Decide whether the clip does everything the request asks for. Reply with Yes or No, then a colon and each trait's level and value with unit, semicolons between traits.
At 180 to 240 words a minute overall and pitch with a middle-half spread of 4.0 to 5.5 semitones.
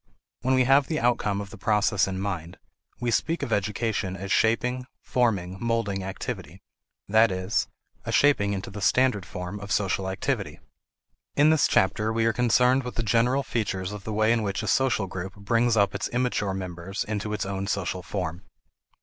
No: average, 185 wpm; average, 3.6 semitones